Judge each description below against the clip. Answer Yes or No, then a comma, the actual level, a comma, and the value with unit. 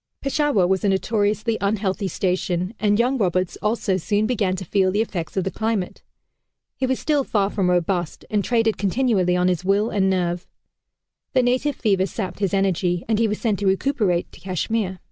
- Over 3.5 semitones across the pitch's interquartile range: No, average, 3.1 semitones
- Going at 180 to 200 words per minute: Yes, average, 185 wpm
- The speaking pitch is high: Yes, high, 200 Hz